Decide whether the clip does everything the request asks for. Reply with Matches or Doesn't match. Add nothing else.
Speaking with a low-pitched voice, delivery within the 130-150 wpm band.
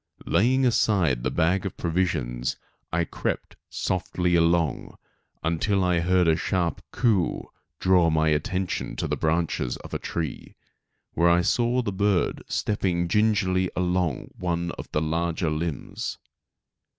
Matches